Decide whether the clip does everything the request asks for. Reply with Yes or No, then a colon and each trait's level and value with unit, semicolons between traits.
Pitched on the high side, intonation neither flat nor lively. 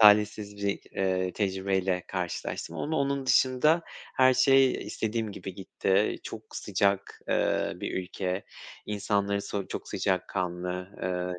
No: low, 100 Hz; average, 3.1 semitones